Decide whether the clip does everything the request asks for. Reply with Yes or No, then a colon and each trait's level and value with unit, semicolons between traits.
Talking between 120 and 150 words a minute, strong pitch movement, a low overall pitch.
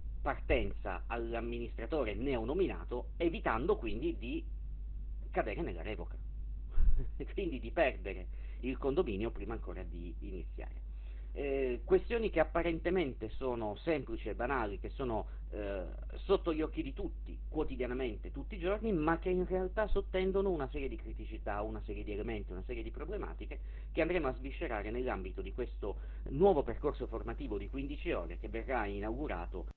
Yes: average, 145 wpm; wide, 8.9 semitones; low, 130 Hz